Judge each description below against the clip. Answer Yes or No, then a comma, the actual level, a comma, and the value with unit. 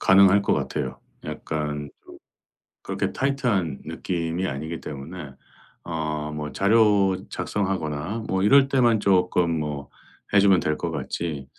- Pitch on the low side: Yes, very low, 90 Hz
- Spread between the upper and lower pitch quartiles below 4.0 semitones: No, average, 4.8 semitones